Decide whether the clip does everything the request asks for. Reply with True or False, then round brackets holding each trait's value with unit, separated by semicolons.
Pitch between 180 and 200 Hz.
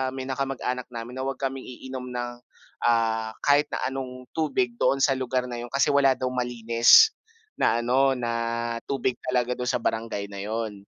False (125 Hz)